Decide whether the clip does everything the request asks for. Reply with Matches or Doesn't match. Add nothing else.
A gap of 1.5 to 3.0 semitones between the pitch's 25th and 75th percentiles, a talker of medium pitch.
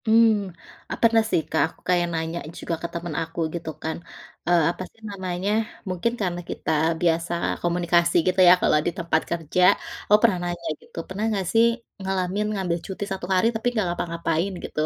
Matches